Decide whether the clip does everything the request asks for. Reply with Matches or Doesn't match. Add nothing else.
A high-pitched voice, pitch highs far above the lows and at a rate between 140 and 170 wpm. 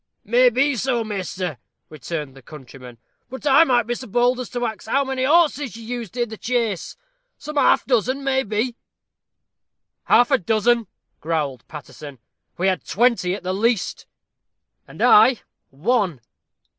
Matches